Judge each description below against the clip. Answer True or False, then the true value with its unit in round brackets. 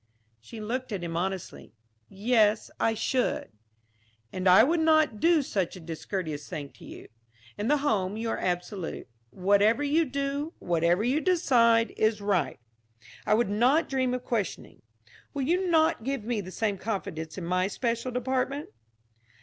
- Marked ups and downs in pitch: True (6.2 semitones)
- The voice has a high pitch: True (225 Hz)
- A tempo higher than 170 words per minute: False (160 wpm)